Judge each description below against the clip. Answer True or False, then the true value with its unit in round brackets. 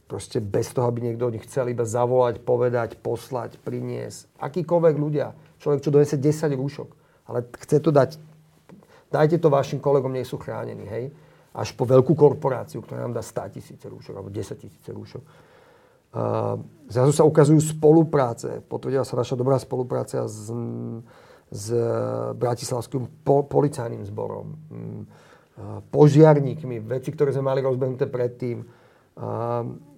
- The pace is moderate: True (135 wpm)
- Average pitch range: True (3.7 semitones)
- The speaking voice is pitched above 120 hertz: True (130 Hz)